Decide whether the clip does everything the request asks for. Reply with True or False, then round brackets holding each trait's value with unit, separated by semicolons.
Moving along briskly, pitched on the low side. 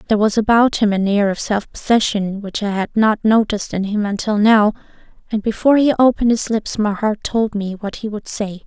False (220 wpm; 210 Hz)